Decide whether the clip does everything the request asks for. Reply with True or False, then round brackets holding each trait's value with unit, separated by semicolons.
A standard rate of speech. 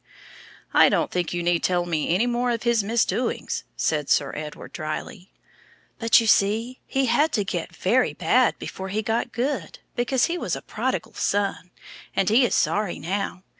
True (175 wpm)